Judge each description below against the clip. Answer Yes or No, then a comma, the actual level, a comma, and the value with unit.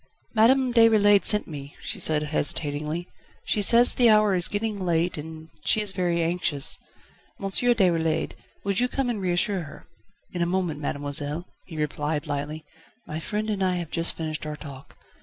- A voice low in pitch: No, medium, 175 Hz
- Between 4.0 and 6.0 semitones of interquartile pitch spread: Yes, average, 5.1 semitones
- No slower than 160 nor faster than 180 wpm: Yes, average, 170 wpm